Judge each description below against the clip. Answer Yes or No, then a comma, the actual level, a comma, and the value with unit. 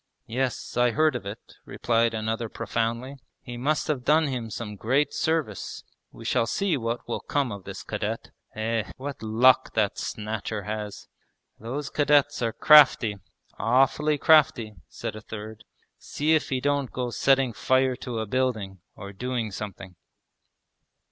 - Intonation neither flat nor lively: Yes, average, 3.8 semitones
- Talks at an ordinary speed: Yes, average, 155 wpm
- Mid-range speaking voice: No, low, 120 Hz